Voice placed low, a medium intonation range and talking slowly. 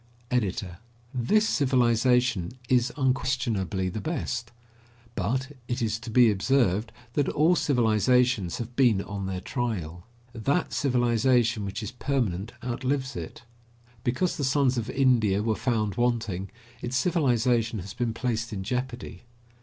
Yes: low, 120 Hz; average, 3.2 semitones; slow, 130 wpm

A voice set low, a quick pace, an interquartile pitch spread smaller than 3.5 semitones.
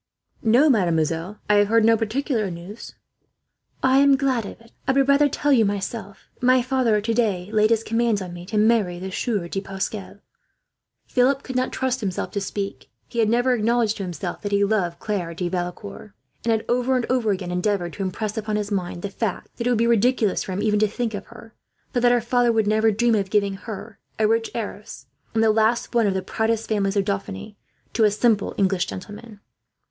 No: high, 215 Hz; fast, 215 wpm; average, 3.1 semitones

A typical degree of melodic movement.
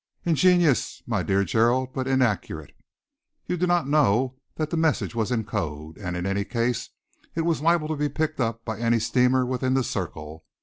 No: wide, 6.4 semitones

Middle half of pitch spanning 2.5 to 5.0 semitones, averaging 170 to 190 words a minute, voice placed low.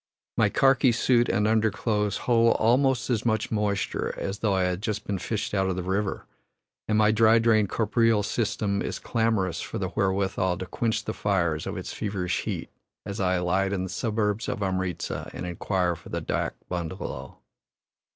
Yes: average, 3.0 semitones; average, 180 wpm; low, 105 Hz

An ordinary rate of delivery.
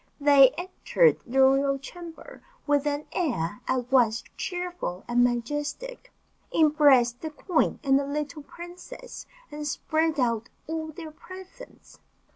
No: slow, 125 wpm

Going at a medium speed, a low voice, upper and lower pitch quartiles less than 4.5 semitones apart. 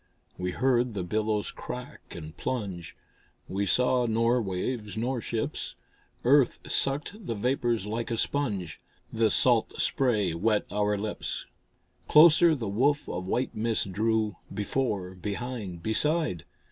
No: slow, 130 wpm; low, 110 Hz; average, 3.9 semitones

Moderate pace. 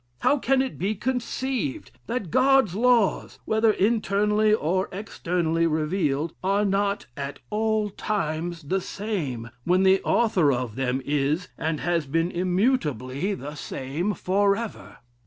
No: slow, 130 wpm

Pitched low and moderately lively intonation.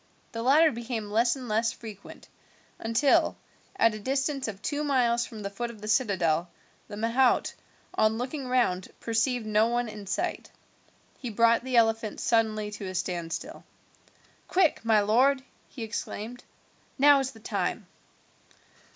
No: high, 230 Hz; average, 3.2 semitones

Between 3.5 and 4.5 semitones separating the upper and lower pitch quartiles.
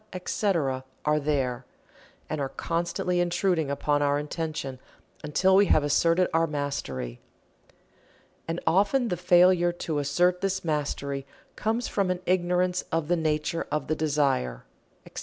Yes: average, 3.8 semitones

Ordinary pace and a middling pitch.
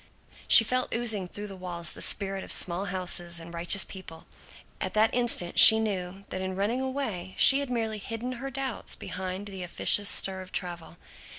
No: average, 185 wpm; high, 195 Hz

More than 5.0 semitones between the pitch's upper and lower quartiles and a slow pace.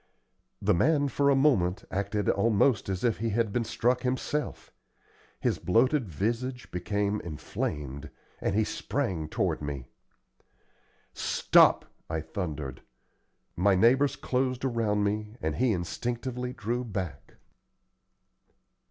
Yes: wide, 5.6 semitones; slow, 115 wpm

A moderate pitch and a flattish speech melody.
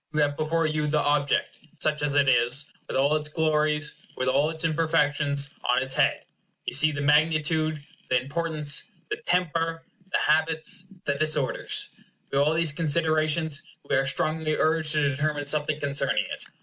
Yes: medium, 150 Hz; narrow, 1.8 semitones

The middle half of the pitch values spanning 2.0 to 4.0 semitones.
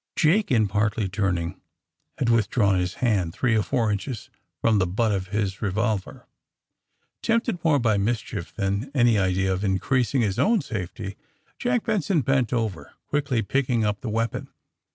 No: average, 4.6 semitones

